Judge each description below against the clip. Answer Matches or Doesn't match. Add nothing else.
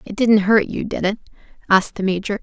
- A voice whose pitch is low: Doesn't match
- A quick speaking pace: Matches